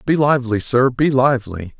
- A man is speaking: Yes, male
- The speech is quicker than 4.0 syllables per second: Yes, 5.5 syllables/s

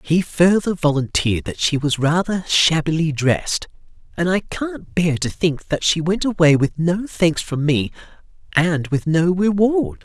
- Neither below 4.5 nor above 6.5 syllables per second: No, 4.3 syllables/s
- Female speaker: No, male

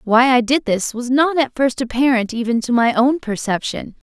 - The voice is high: Yes, very high, 250 Hz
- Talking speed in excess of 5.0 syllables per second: No, 4.9 syllables/s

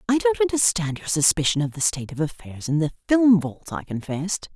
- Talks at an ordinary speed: No, fast, 210 wpm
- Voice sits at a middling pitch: Yes, medium, 170 Hz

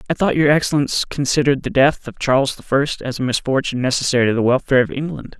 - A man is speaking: Yes, male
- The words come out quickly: Yes, fast, 225 wpm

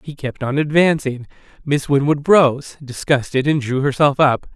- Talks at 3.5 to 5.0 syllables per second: Yes, 4.5 syllables/s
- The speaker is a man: Yes, male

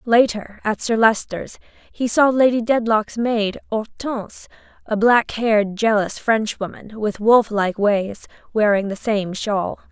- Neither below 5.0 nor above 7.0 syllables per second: No, 4.1 syllables/s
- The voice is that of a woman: Yes, female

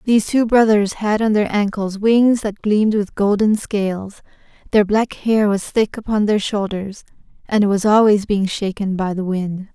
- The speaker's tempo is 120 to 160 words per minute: No, average, 185 wpm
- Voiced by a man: No, female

